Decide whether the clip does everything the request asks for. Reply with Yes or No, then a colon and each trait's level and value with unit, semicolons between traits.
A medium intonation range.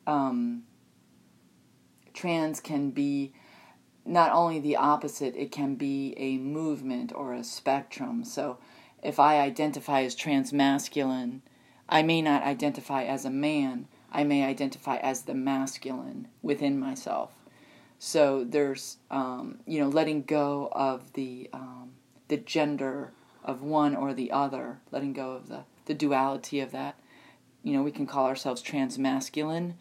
No: narrow, 1.9 semitones